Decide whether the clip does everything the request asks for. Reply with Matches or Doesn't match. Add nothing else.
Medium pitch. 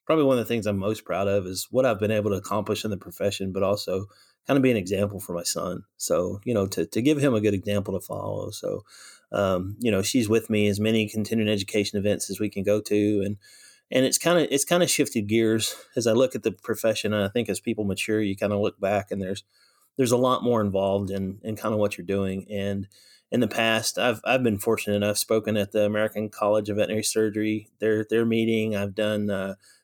Doesn't match